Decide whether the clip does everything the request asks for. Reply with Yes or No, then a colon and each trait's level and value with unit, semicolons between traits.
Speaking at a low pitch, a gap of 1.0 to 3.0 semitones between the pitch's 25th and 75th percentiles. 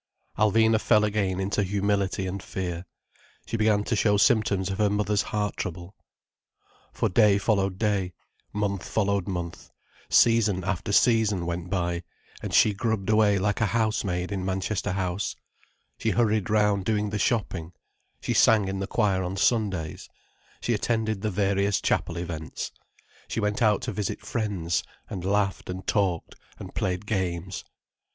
Yes: low, 100 Hz; narrow, 2.4 semitones